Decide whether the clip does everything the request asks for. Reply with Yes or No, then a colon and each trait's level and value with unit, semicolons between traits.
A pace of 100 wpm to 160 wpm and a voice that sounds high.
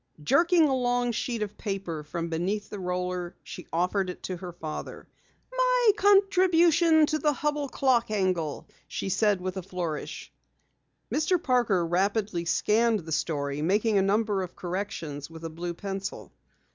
Yes: average, 155 wpm; high, 195 Hz